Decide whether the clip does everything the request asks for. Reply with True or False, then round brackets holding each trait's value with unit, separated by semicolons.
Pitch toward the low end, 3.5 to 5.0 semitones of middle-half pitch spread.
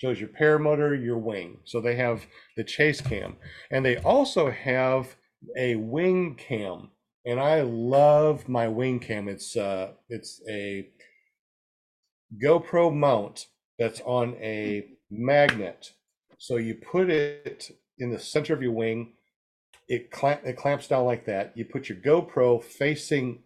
True (125 Hz; 4.2 semitones)